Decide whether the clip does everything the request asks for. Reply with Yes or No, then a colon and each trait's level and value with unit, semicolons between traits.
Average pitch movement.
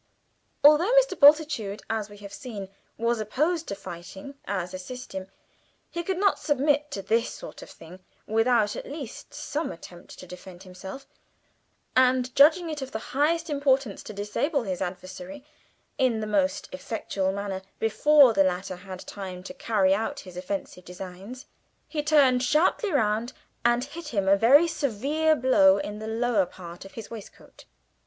No: wide, 6.7 semitones